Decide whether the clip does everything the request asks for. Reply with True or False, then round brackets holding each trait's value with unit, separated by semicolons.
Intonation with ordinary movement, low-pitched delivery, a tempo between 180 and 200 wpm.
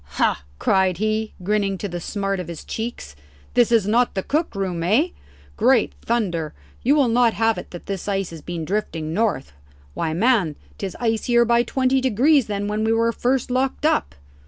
False (4.2 semitones; 215 Hz; 185 wpm)